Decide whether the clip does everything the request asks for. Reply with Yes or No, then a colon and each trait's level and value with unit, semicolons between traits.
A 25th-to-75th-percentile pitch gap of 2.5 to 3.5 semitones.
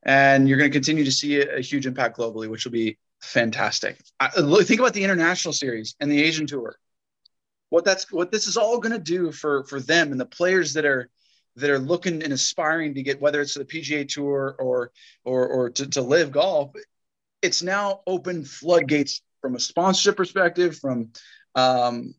No: average, 4.7 semitones